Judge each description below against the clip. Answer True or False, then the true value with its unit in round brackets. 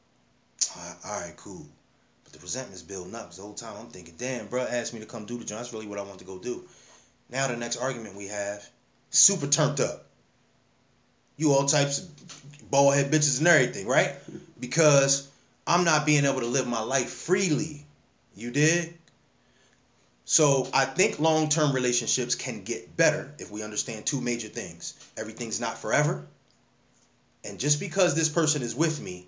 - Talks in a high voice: False (135 Hz)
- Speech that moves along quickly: False (180 wpm)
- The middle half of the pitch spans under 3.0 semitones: False (4.9 semitones)